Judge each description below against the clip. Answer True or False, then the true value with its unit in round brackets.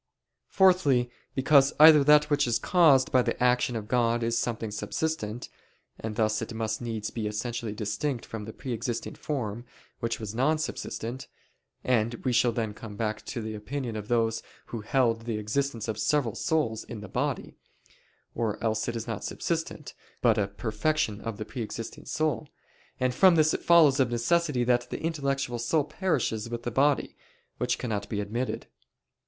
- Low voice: True (120 Hz)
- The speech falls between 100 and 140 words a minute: False (175 wpm)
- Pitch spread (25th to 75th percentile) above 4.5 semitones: False (3.9 semitones)